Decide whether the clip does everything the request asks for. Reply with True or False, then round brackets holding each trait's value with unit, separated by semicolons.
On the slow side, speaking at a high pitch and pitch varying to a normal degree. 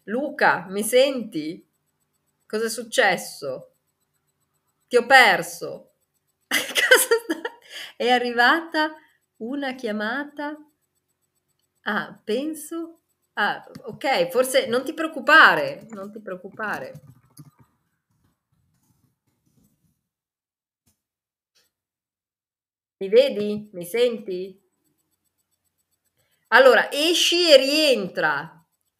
False (70 wpm; 265 Hz; 6.6 semitones)